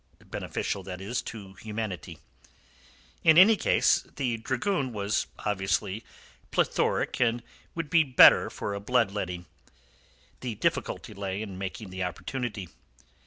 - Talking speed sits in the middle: No, slow, 130 wpm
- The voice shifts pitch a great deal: No, average, 4.5 semitones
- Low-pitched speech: Yes, low, 105 Hz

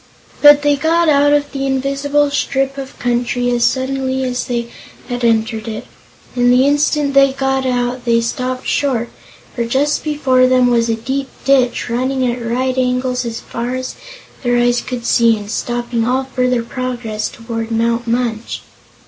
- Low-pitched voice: No, very high, 250 Hz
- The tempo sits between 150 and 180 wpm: Yes, average, 165 wpm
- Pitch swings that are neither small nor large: No, narrow, 2.2 semitones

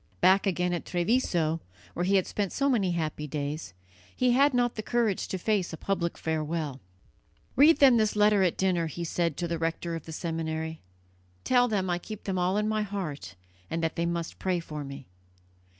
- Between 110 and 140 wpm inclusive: No, average, 200 wpm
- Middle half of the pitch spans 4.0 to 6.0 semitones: Yes, average, 4.4 semitones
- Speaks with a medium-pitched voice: Yes, medium, 175 Hz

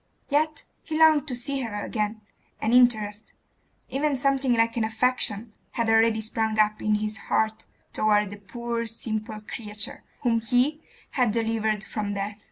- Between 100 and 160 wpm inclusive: Yes, average, 155 wpm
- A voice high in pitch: Yes, high, 225 Hz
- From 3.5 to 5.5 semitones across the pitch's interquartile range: No, narrow, 2.6 semitones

